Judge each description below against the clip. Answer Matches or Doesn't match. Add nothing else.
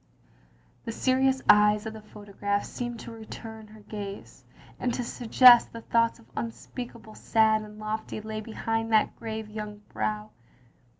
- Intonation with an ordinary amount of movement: Doesn't match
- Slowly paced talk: Doesn't match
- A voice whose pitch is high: Matches